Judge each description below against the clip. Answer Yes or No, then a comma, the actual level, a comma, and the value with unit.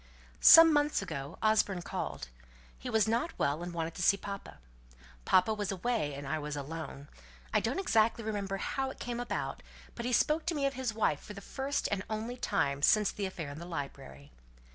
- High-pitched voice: Yes, high, 200 Hz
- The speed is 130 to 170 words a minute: No, average, 200 wpm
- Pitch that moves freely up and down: Yes, wide, 7.3 semitones